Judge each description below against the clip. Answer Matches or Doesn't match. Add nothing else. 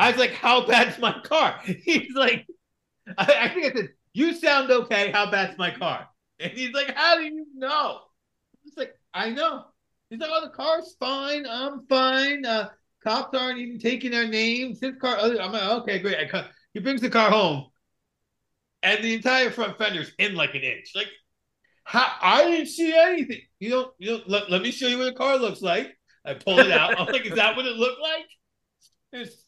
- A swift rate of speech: Matches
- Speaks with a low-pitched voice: Doesn't match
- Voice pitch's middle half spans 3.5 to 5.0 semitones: Matches